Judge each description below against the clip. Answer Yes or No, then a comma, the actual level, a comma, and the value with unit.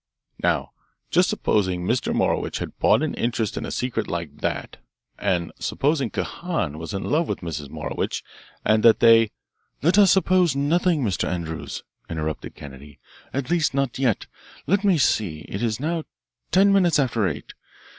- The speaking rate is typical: Yes, average, 165 wpm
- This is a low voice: Yes, low, 120 Hz